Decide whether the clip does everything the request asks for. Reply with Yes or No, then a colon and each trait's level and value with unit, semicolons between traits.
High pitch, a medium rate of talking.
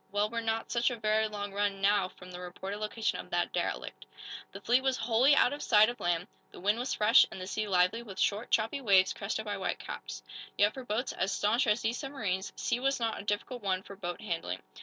No: high, 210 Hz; fast, 235 wpm